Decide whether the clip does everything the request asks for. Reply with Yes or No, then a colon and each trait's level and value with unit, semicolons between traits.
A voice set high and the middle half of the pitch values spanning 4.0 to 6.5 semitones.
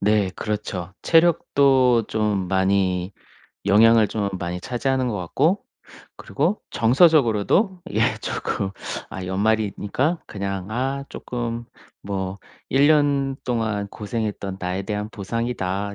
No: low, 110 Hz; average, 5.1 semitones